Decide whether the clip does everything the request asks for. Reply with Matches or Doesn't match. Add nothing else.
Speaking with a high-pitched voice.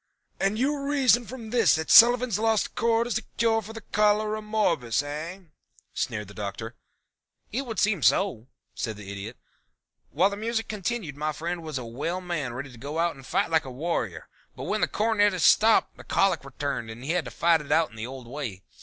Doesn't match